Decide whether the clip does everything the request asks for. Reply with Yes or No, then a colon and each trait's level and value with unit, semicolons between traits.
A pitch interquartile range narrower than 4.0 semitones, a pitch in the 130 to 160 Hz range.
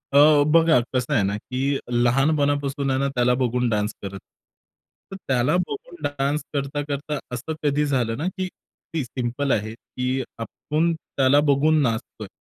Yes: average, 3.2 semitones; medium, 140 Hz